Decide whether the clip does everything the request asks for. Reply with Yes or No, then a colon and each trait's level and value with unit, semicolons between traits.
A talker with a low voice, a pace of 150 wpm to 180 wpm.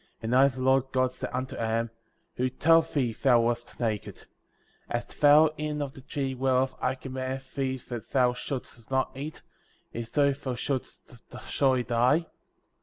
Yes: low, 130 Hz; average, 175 wpm